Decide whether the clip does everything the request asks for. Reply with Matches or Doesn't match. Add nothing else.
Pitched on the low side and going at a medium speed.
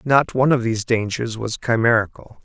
Matches